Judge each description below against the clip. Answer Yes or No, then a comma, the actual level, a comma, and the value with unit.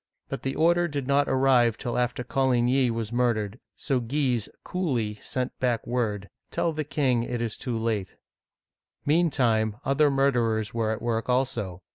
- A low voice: Yes, low, 125 Hz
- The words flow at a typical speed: Yes, average, 165 wpm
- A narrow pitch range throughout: No, average, 3.2 semitones